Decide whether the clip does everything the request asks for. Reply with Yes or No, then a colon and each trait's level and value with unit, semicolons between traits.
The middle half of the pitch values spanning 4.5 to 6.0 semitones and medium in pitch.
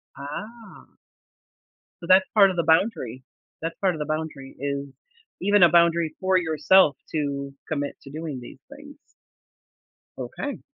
Yes: average, 4.9 semitones; medium, 160 Hz